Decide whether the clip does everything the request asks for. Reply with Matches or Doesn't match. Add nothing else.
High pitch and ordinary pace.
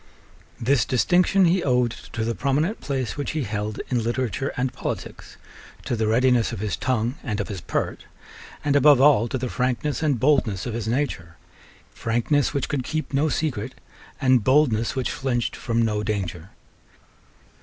Doesn't match